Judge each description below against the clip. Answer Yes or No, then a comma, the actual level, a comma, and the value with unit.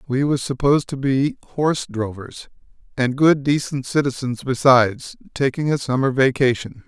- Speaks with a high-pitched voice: No, low, 135 Hz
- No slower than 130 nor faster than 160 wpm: Yes, average, 140 wpm